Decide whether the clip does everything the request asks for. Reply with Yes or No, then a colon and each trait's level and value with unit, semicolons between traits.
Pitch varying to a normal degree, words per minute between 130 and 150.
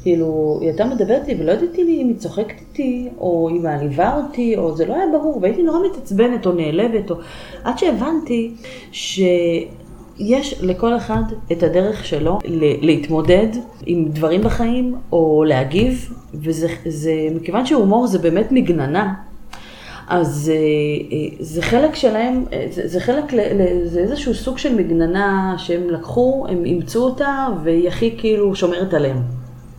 No: wide, 6.7 semitones; average, 145 wpm